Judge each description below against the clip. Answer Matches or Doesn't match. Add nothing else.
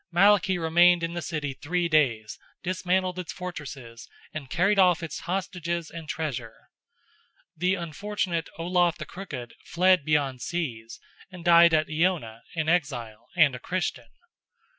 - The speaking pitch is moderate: Matches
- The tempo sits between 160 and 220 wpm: Doesn't match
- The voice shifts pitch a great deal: Doesn't match